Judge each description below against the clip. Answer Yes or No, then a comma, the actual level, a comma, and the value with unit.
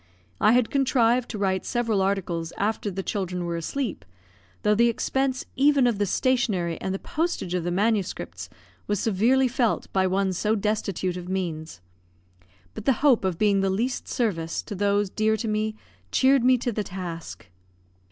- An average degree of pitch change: Yes, average, 4.3 semitones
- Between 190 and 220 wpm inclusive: No, average, 175 wpm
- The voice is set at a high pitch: Yes, high, 205 Hz